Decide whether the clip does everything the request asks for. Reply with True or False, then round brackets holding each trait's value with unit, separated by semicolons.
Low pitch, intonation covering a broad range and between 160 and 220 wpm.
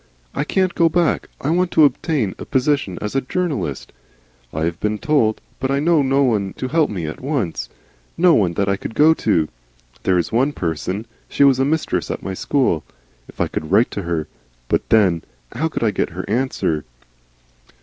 True (120 Hz; 7.9 semitones; 200 wpm)